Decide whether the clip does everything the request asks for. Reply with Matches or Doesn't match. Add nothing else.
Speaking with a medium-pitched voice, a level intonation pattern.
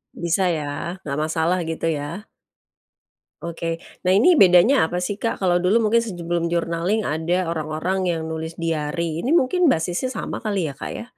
Doesn't match